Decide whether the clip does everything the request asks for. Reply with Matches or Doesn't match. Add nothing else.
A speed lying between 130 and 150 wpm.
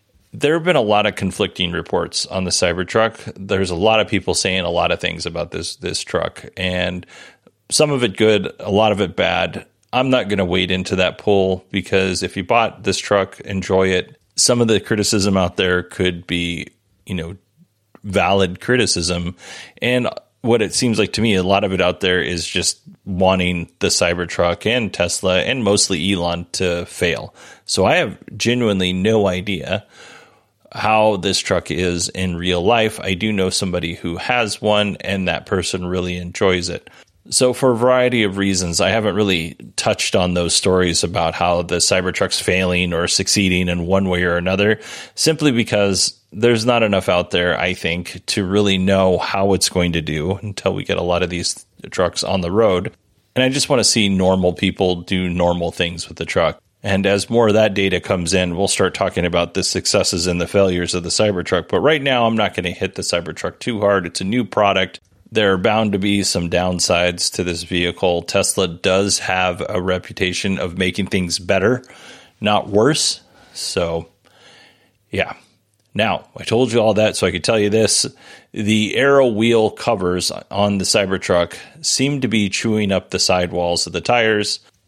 Doesn't match